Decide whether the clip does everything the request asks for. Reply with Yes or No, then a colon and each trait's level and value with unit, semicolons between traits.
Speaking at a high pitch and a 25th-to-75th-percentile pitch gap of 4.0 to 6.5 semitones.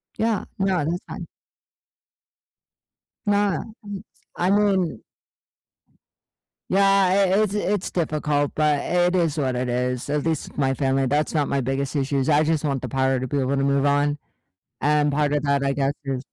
No: medium, 145 Hz; average, 4.5 semitones